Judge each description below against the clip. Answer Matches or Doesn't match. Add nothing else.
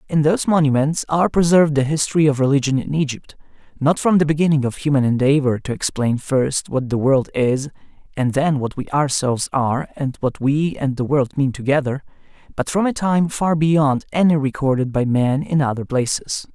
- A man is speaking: Matches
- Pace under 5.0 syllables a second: Doesn't match